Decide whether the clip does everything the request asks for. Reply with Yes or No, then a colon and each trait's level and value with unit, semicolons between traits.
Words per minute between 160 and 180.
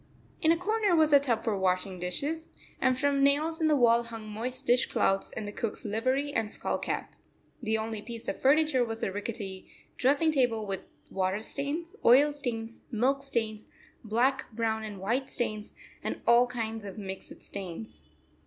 Yes: average, 175 wpm